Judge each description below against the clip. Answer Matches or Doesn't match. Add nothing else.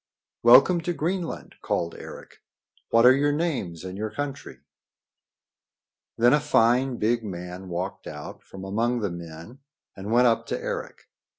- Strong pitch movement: Matches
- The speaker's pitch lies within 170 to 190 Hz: Doesn't match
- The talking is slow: Doesn't match